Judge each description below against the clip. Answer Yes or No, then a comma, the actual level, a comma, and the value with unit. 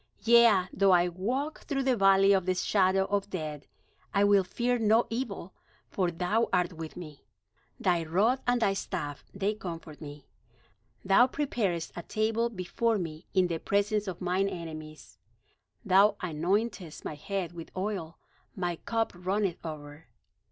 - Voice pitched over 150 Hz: Yes, high, 190 Hz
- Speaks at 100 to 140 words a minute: No, average, 150 wpm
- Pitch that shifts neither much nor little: Yes, average, 3.9 semitones